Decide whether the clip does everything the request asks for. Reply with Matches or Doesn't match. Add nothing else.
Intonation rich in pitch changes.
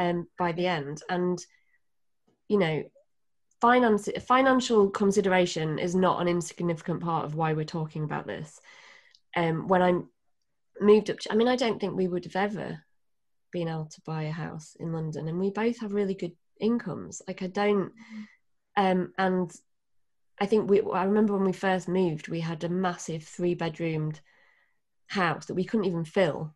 Doesn't match